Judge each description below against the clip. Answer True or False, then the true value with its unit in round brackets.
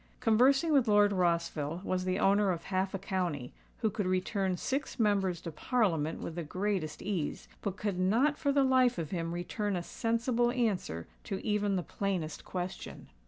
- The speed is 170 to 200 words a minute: True (175 wpm)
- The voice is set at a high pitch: True (195 Hz)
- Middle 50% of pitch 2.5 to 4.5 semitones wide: True (4.2 semitones)